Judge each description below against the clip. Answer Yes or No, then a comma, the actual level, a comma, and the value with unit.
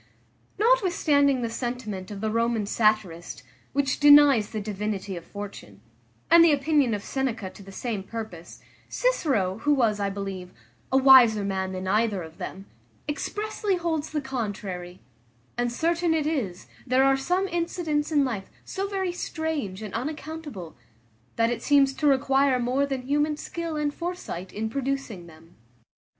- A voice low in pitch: No, very high, 255 Hz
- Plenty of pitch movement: Yes, wide, 6.6 semitones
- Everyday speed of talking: Yes, average, 155 wpm